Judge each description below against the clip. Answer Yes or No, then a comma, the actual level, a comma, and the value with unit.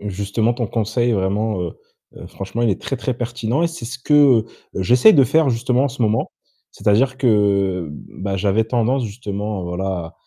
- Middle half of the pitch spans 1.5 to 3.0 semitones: No, average, 4.0 semitones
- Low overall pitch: Yes, low, 110 Hz